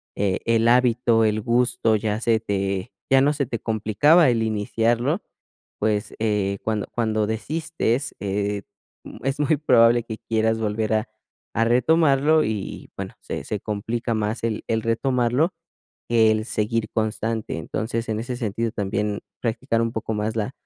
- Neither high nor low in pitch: No, low, 115 Hz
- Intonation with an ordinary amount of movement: No, narrow, 2.1 semitones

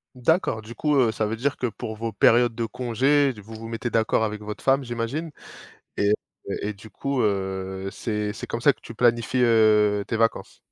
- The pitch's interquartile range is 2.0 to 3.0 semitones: Yes, narrow, 2.5 semitones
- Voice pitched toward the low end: Yes, low, 115 Hz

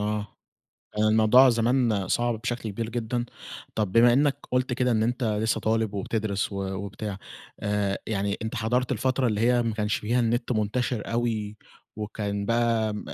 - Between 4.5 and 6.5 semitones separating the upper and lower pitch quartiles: No, narrow, 2.4 semitones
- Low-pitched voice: Yes, low, 110 Hz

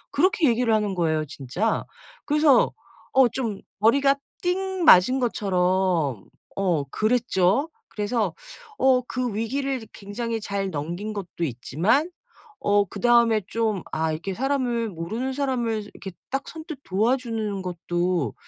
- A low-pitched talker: No, high, 220 Hz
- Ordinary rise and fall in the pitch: No, wide, 5.8 semitones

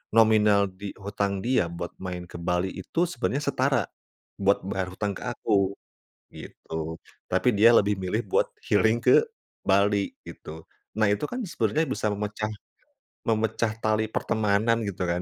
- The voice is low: Yes, low, 105 Hz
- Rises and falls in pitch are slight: Yes, narrow, 2.2 semitones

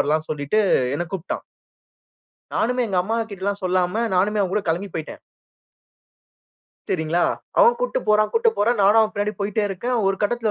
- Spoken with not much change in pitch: No, average, 3.5 semitones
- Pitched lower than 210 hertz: Yes, high, 200 Hz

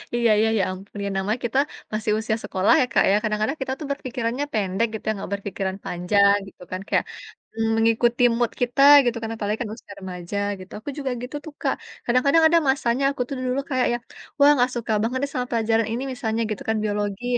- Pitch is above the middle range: Yes, high, 225 Hz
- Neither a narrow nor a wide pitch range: Yes, average, 3.5 semitones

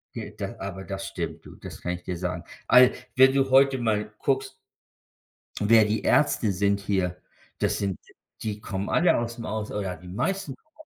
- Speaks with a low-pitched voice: Yes, low, 105 Hz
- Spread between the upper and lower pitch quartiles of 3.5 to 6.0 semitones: Yes, average, 5.1 semitones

